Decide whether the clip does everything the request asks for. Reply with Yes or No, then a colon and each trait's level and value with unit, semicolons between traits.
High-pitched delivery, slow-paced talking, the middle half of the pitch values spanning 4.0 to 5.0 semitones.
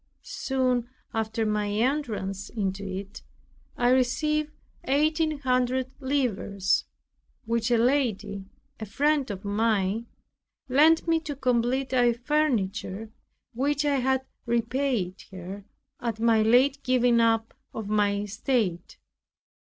Yes: high, 235 Hz; slow, 115 wpm; average, 4.3 semitones